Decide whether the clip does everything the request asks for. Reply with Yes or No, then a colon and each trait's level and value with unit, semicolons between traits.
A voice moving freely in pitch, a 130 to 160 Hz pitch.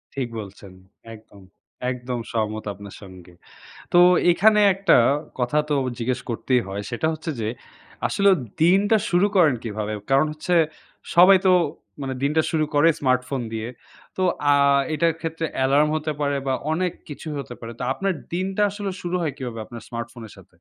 Yes: wide, 6.5 semitones; medium, 140 Hz